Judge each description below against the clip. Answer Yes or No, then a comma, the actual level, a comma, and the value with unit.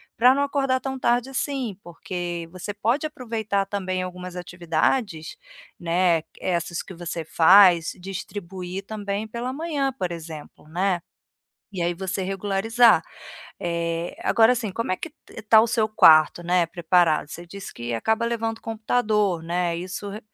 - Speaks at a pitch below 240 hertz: Yes, high, 190 Hz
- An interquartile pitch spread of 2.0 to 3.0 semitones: No, average, 4.6 semitones